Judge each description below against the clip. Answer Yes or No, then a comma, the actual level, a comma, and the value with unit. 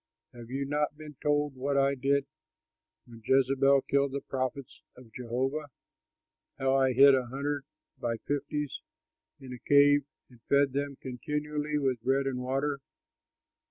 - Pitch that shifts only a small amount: Yes, narrow, 1.8 semitones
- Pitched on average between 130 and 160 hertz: Yes, low, 135 Hz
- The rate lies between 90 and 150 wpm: Yes, average, 145 wpm